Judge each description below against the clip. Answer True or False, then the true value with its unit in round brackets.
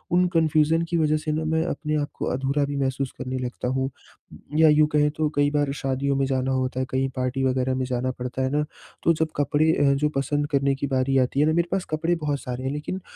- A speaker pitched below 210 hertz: True (140 Hz)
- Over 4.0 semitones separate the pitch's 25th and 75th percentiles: False (2.6 semitones)